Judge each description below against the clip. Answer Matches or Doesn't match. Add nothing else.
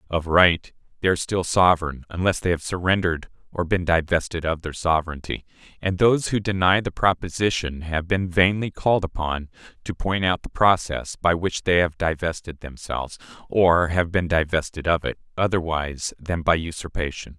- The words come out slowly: Doesn't match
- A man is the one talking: Matches